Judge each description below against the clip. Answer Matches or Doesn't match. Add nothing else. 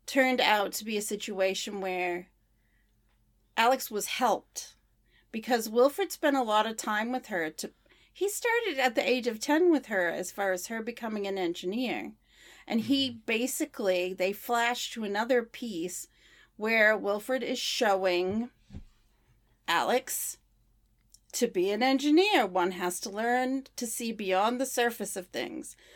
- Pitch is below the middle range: Doesn't match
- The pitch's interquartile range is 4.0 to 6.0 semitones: Matches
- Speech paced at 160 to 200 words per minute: Doesn't match